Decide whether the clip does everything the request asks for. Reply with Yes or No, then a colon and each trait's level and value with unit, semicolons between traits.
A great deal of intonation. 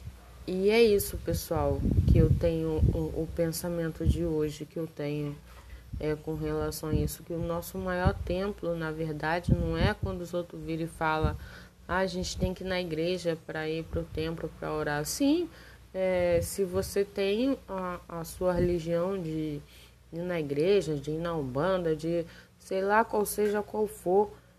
No: average, 3.0 semitones